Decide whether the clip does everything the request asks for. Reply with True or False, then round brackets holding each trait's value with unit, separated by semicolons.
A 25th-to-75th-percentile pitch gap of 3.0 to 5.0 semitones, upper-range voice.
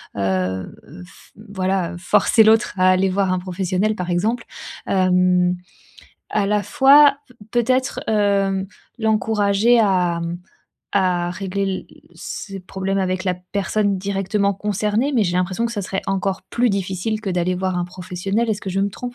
False (2.5 semitones; 195 Hz)